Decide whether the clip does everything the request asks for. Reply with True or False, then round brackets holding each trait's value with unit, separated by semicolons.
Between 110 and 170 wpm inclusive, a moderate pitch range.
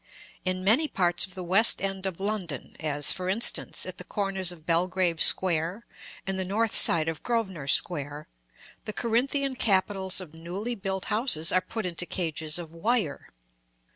True (165 wpm; 3.7 semitones)